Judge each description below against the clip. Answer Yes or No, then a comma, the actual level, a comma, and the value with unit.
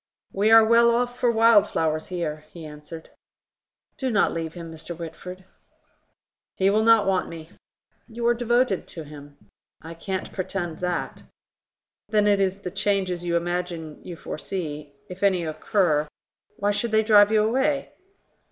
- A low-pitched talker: No, medium, 185 Hz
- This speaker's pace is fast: No, average, 155 wpm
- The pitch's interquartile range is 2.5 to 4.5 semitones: No, average, 4.9 semitones